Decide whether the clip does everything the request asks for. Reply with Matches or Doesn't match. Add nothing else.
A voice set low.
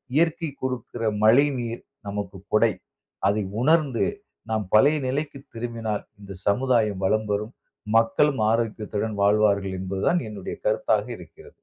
Matches